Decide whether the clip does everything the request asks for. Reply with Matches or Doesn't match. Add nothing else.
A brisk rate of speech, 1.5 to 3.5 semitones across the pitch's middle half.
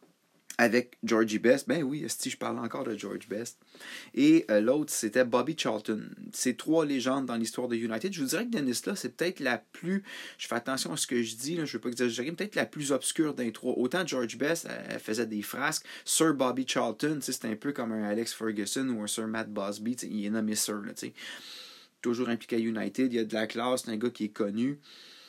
Doesn't match